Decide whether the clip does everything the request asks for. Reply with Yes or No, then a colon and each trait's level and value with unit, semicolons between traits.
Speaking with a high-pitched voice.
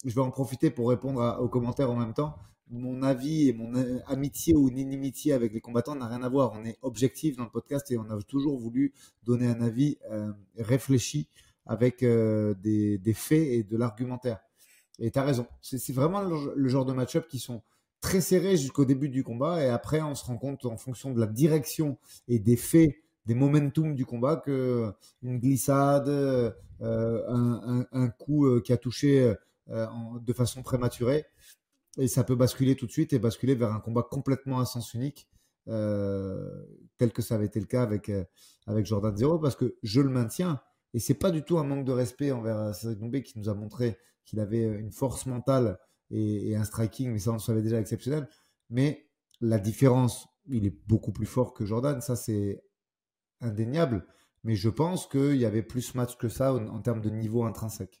No: low, 125 Hz